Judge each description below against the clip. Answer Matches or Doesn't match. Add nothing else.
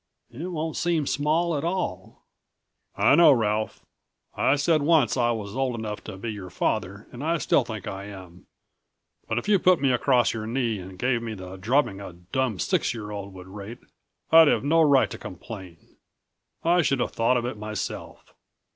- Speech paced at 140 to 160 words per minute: Doesn't match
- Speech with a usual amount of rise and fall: Doesn't match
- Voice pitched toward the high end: Doesn't match